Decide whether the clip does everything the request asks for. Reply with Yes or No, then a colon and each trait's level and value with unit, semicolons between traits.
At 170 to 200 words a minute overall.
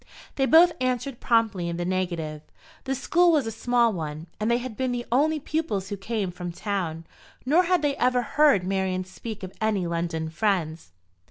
Yes: average, 185 wpm